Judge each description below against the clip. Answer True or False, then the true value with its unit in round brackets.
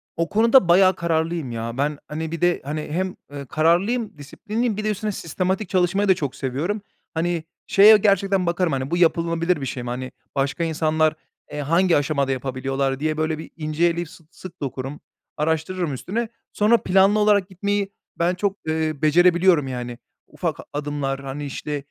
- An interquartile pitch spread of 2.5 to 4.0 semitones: False (4.4 semitones)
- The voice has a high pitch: False (165 Hz)